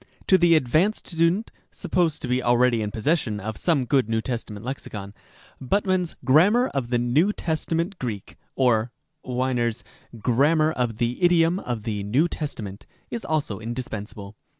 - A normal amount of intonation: No, wide, 6.4 semitones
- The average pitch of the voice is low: Yes, low, 130 Hz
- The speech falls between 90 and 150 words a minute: No, average, 170 wpm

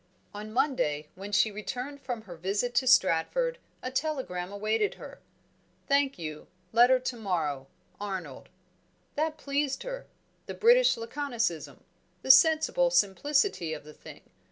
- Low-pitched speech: No, high, 235 Hz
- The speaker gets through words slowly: Yes, slow, 130 wpm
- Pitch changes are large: Yes, wide, 7.7 semitones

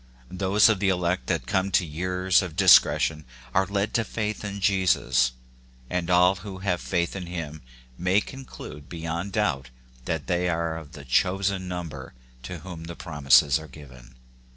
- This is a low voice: Yes, very low, 90 Hz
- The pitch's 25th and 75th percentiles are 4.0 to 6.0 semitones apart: No, average, 3.6 semitones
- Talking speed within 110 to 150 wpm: No, average, 170 wpm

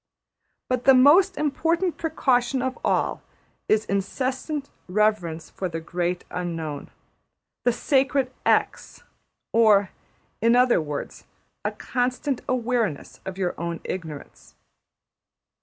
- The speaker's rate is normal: No, slow, 110 wpm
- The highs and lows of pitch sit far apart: Yes, wide, 6.7 semitones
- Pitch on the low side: No, high, 230 Hz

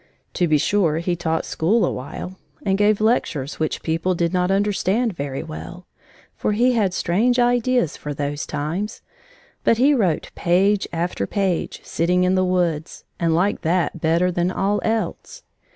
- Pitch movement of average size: Yes, average, 4.1 semitones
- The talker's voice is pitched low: No, medium, 180 Hz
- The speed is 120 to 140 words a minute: No, average, 165 wpm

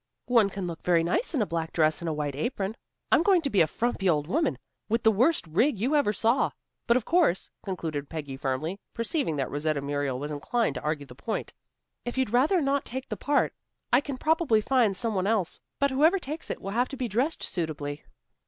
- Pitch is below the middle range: No, high, 210 Hz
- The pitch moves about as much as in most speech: No, wide, 8.9 semitones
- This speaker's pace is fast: Yes, fast, 220 wpm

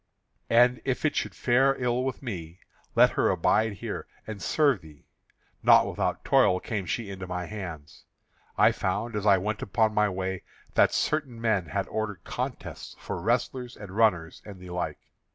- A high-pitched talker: No, low, 105 Hz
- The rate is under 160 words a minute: No, average, 170 wpm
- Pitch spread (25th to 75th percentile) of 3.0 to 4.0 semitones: No, average, 4.7 semitones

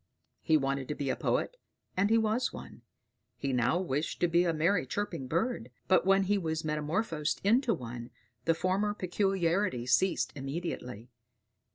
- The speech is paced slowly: No, average, 160 wpm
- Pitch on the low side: No, medium, 170 Hz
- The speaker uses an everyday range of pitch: No, wide, 6.1 semitones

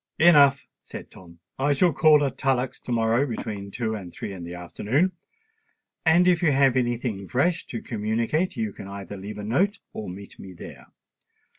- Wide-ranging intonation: Yes, wide, 6.0 semitones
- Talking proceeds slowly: No, average, 185 wpm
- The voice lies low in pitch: Yes, low, 120 Hz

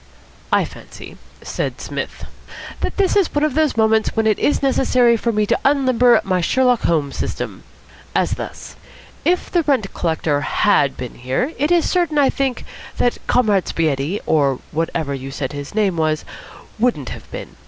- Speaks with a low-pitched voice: No, high, 220 Hz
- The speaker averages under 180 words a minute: Yes, average, 170 wpm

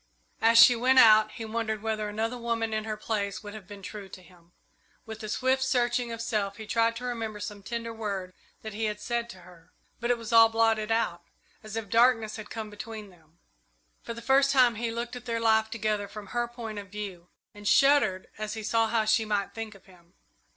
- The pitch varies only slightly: Yes, narrow, 1.9 semitones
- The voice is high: Yes, high, 220 Hz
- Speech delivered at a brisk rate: Yes, fast, 220 wpm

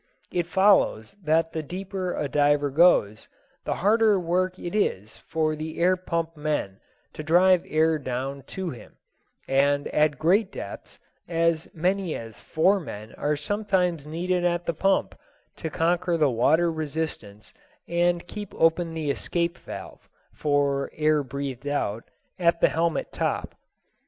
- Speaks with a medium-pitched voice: Yes, medium, 160 Hz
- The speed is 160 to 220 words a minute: No, average, 145 wpm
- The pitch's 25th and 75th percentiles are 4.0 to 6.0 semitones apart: No, average, 3.6 semitones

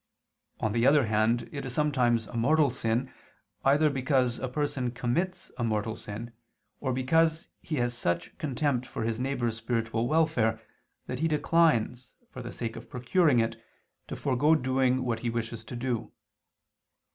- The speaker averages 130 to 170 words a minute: Yes, average, 160 wpm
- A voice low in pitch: Yes, low, 125 Hz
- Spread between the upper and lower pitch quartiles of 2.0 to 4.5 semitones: Yes, average, 3.6 semitones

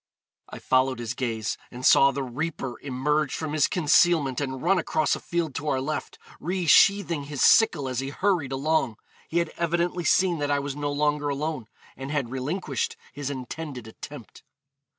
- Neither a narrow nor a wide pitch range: Yes, average, 3.4 semitones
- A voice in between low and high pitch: Yes, medium, 145 Hz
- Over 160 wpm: Yes, average, 170 wpm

